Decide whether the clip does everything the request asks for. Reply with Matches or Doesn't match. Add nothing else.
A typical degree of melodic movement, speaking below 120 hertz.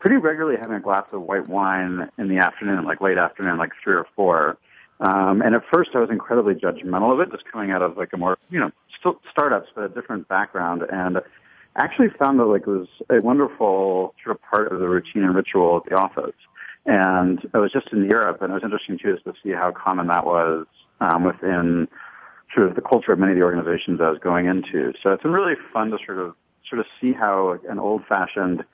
Doesn't match